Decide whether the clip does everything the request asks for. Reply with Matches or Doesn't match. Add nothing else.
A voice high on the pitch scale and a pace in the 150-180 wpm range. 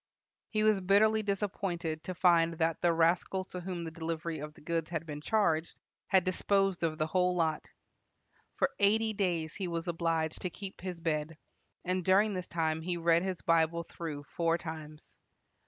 Doesn't match